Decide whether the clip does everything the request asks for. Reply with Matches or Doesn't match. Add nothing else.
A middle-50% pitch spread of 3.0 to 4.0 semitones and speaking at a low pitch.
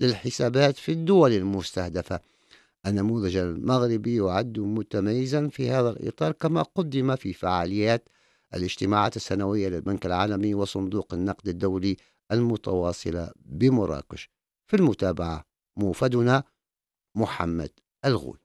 Doesn't match